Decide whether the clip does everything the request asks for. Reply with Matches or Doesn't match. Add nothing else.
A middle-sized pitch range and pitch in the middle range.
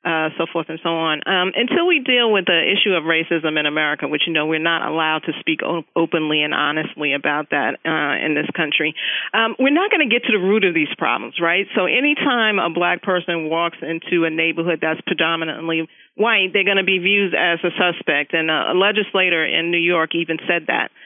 Matches